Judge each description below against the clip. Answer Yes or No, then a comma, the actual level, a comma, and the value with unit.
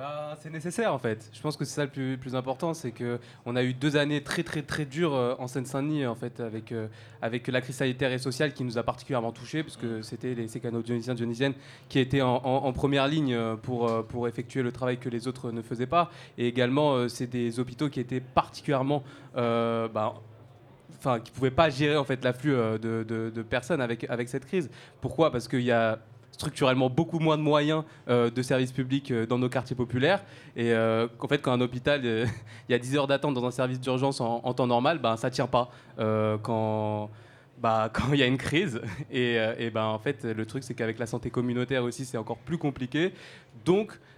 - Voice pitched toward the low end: Yes, low, 125 Hz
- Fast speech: Yes, fast, 225 wpm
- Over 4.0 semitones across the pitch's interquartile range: No, average, 2.8 semitones